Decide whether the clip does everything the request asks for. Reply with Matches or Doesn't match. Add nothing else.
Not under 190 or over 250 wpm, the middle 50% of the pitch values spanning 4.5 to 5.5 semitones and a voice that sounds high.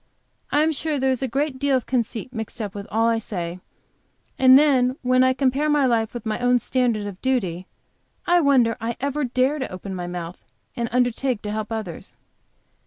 Doesn't match